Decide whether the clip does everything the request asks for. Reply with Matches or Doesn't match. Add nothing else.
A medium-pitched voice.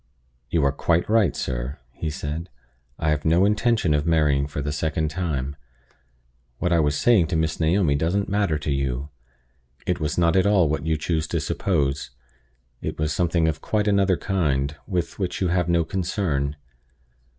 Doesn't match